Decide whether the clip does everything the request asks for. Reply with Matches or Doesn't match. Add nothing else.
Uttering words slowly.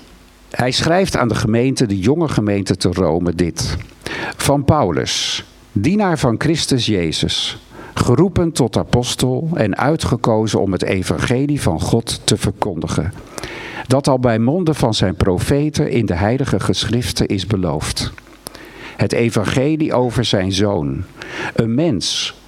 Matches